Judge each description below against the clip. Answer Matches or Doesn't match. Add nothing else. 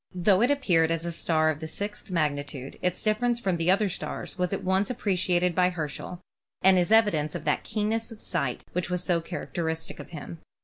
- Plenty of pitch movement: Doesn't match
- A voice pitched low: Doesn't match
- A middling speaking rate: Doesn't match